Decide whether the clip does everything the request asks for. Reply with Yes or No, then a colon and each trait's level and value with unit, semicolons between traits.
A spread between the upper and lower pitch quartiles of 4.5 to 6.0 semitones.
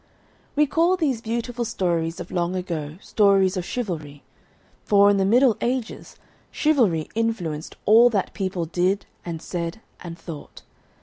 Yes: average, 5.2 semitones